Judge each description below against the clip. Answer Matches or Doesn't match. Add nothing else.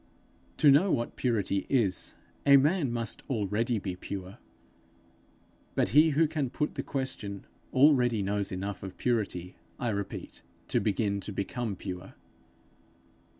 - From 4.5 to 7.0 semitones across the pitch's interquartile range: Matches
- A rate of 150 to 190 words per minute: Doesn't match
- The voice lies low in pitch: Matches